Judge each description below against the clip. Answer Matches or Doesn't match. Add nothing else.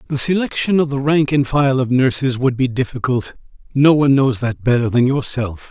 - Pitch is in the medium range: Doesn't match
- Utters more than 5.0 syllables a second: Matches